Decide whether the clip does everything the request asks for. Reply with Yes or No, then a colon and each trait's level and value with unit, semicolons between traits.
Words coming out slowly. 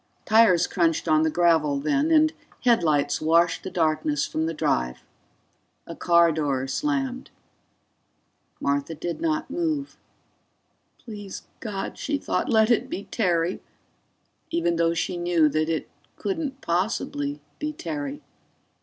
Yes: slow, 125 wpm